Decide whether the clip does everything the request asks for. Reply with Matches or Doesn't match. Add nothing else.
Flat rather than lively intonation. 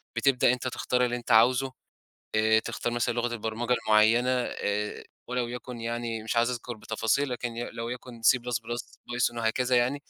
Matches